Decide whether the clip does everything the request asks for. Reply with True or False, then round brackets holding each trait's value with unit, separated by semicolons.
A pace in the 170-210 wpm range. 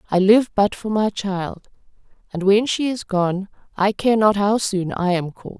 True (205 wpm)